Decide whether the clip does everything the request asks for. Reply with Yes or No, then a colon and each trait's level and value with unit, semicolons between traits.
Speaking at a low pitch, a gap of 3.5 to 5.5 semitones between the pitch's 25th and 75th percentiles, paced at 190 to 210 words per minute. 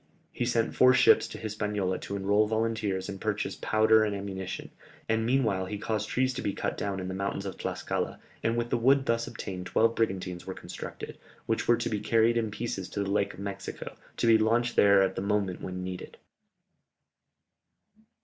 No: low, 105 Hz; average, 2.8 semitones; average, 195 wpm